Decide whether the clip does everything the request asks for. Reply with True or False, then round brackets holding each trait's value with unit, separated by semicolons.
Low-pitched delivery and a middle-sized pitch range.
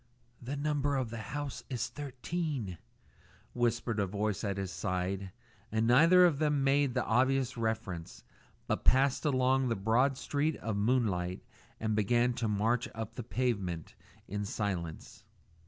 True (120 Hz; 4.9 semitones)